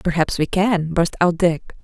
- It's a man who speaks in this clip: No, female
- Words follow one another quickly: No, average, 195 wpm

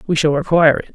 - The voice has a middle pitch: Yes, medium, 155 Hz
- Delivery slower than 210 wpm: No, fast, 255 wpm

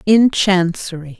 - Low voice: No, medium, 185 Hz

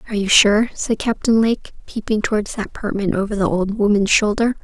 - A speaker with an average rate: Yes, average, 195 wpm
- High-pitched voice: Yes, high, 210 Hz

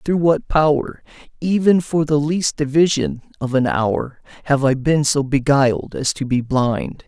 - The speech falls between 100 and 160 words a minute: No, average, 170 wpm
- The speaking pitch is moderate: Yes, medium, 145 Hz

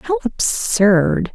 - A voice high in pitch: Yes, high, 240 Hz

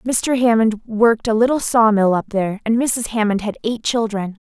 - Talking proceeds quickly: No, average, 190 wpm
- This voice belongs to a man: No, female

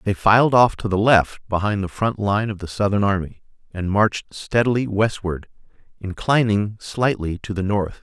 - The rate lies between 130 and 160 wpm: No, average, 170 wpm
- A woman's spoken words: No, male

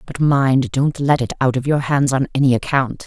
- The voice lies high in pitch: No, low, 135 Hz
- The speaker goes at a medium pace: No, fast, 235 wpm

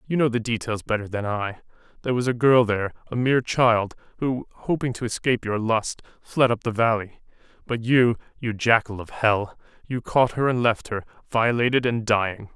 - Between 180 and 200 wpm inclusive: Yes, average, 190 wpm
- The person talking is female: No, male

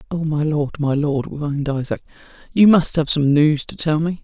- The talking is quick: Yes, fast, 215 wpm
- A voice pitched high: No, medium, 150 Hz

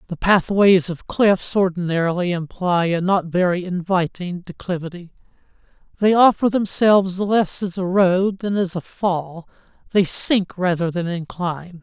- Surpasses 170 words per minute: No, slow, 135 wpm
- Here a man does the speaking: Yes, male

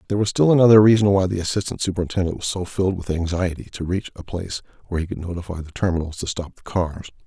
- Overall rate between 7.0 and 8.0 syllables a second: Yes, 7.1 syllables/s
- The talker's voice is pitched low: Yes, very low, 90 Hz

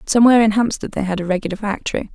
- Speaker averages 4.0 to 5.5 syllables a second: No, 8.0 syllables/s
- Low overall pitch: No, high, 210 Hz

